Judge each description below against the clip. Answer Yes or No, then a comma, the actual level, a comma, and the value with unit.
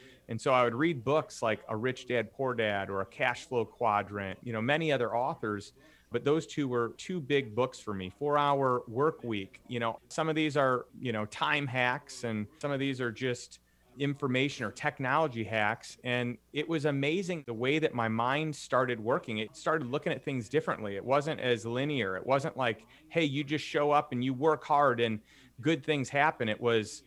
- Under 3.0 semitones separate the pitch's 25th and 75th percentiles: No, average, 4.3 semitones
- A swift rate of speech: Yes, fast, 210 wpm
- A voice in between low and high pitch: No, low, 130 Hz